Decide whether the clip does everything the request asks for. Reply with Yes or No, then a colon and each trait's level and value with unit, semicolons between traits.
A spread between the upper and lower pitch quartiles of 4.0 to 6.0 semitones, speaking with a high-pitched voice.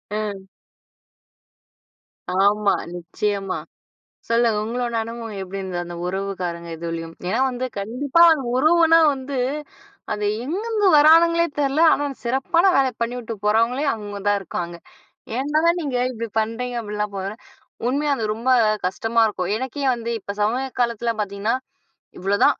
Yes: average, 4.8 semitones; high, 230 Hz